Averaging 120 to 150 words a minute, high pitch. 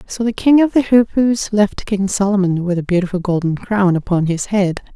No: fast, 205 wpm; high, 200 Hz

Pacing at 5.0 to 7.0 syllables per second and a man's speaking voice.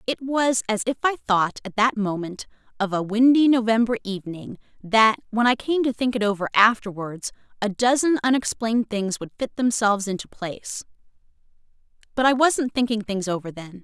No: 5.3 syllables/s; female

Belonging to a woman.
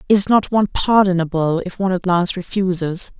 Yes: female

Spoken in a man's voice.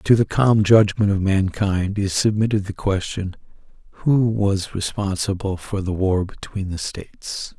Yes: male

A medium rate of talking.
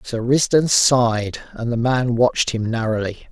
Yes: average, 165 wpm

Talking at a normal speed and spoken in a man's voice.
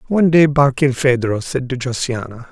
Yes: average, 145 wpm; male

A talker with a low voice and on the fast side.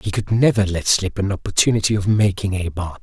Yes: low, 100 Hz; fast, 220 wpm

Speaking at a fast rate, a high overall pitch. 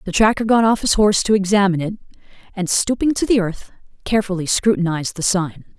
No: average, 185 wpm; high, 200 Hz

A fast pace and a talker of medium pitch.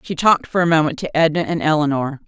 Yes: fast, 240 wpm; medium, 155 Hz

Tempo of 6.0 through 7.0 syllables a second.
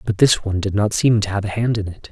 Yes: 6.6 syllables/s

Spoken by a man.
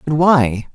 Yes: male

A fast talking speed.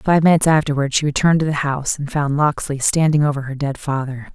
Yes: fast, 220 wpm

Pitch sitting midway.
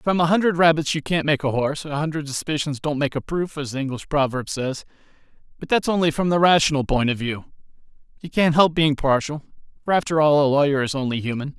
Yes: medium, 150 Hz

